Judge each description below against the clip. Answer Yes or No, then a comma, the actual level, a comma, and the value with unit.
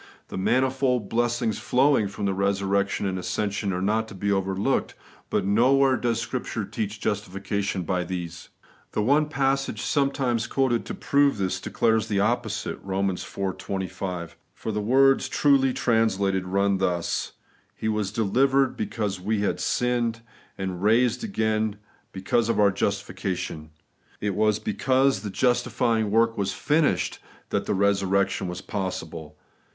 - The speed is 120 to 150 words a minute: Yes, average, 145 wpm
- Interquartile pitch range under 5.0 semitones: Yes, average, 3.9 semitones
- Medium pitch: No, low, 105 Hz